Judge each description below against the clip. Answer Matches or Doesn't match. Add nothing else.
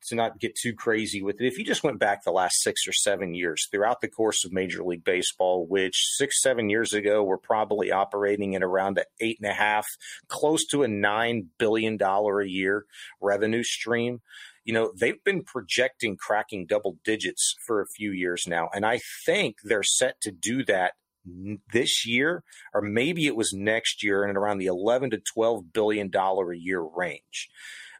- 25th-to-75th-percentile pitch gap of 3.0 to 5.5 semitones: Doesn't match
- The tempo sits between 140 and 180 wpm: Doesn't match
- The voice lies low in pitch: Matches